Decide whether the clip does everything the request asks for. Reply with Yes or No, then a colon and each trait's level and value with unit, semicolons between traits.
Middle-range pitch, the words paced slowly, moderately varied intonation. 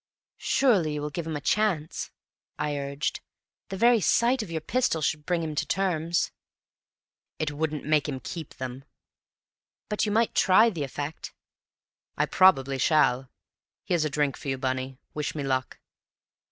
No: medium, 155 Hz; average, 160 wpm; average, 4.8 semitones